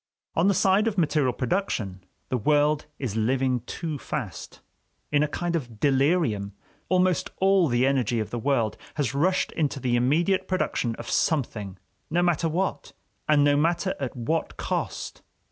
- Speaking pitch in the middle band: Yes, medium, 145 Hz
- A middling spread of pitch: No, wide, 5.8 semitones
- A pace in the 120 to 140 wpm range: No, average, 160 wpm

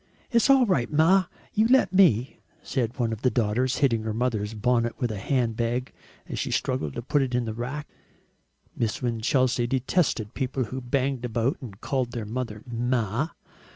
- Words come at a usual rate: Yes, average, 165 wpm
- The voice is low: Yes, low, 125 Hz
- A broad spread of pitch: No, average, 2.7 semitones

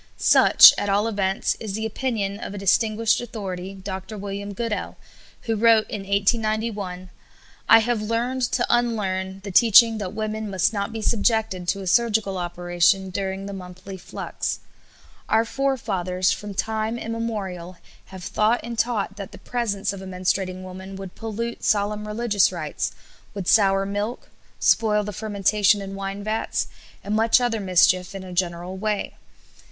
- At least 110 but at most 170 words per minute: Yes, average, 155 wpm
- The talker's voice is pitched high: Yes, high, 205 Hz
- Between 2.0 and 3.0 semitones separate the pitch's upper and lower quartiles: Yes, average, 2.7 semitones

